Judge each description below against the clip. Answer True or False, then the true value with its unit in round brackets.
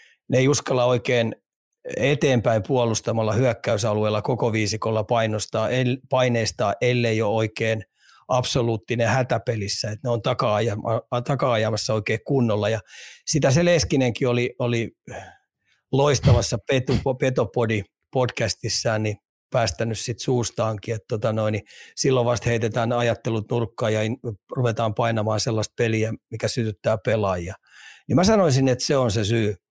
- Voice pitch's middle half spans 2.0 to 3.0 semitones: True (2.5 semitones)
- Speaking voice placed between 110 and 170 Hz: True (115 Hz)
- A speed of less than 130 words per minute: True (120 wpm)